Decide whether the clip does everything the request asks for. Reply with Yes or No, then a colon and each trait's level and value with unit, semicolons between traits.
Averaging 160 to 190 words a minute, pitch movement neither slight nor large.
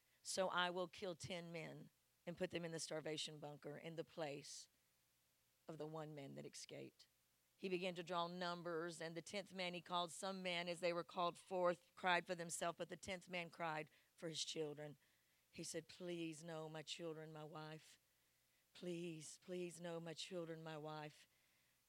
No: average, 180 wpm; narrow, 2.3 semitones